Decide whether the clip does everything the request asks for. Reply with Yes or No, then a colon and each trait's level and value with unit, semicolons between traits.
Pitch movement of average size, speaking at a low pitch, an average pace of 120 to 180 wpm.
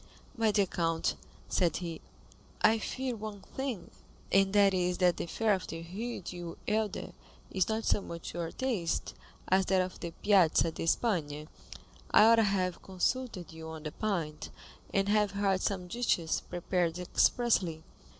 No: average, 3.8 semitones; medium, 185 Hz; average, 165 wpm